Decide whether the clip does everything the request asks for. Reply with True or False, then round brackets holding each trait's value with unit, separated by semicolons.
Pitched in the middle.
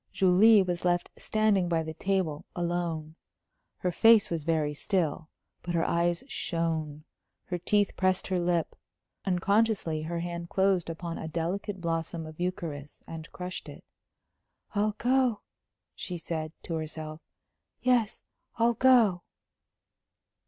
True (175 Hz)